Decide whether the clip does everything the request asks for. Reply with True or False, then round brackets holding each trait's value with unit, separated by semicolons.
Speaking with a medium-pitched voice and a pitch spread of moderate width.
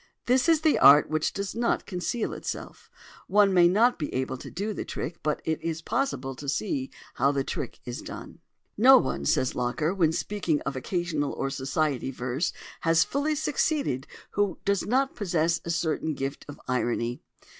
False (165 Hz; 7.0 semitones)